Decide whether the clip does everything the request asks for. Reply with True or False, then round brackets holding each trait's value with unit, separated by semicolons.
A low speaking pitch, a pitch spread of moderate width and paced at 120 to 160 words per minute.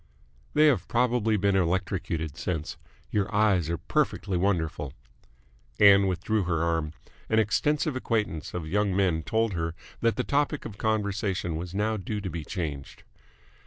True (100 Hz; 4.3 semitones; 150 wpm)